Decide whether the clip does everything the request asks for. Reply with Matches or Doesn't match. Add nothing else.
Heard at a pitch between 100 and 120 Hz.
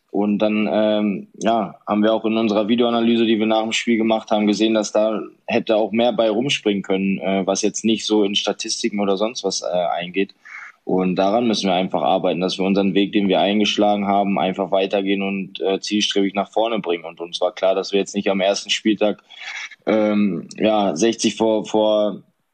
Matches